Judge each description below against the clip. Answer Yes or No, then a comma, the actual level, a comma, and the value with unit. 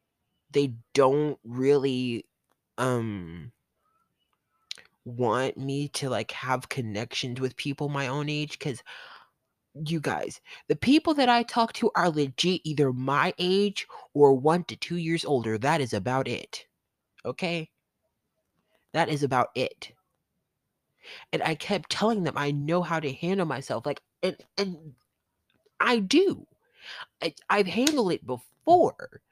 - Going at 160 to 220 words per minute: No, slow, 135 wpm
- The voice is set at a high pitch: No, medium, 145 Hz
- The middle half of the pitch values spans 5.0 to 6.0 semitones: Yes, average, 5.3 semitones